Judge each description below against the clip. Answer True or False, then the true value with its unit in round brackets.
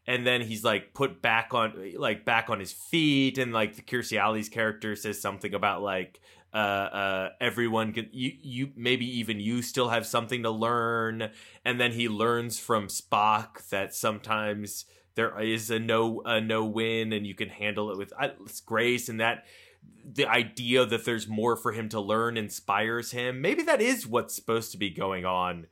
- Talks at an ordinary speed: True (185 wpm)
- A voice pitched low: True (110 Hz)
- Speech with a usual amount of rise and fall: False (2.2 semitones)